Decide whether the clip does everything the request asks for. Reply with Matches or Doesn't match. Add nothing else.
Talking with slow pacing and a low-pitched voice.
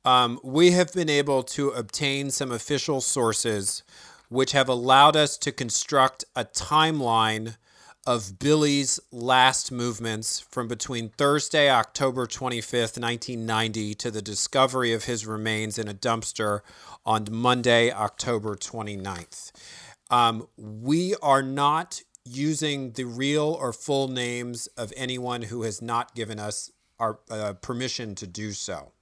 Matches